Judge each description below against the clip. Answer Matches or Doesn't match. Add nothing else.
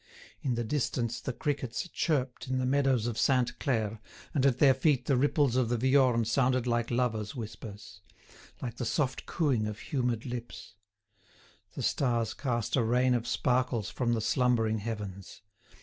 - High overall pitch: Doesn't match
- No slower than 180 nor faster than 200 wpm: Doesn't match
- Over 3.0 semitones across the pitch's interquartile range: Doesn't match